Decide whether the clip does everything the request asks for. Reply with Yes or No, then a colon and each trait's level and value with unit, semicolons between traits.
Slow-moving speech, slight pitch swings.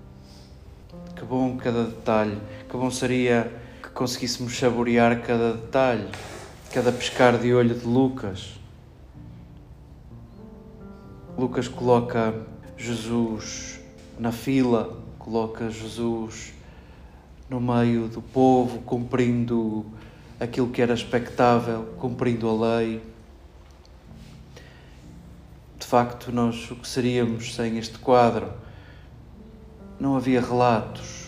Yes: slow, 90 wpm; narrow, 2.1 semitones